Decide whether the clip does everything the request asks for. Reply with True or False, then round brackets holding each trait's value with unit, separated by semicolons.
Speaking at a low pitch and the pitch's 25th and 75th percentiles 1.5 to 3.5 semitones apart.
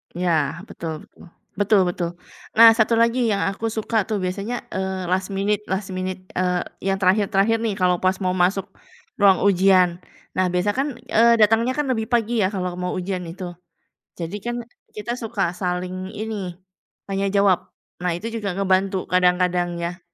False (190 Hz; 2.7 semitones)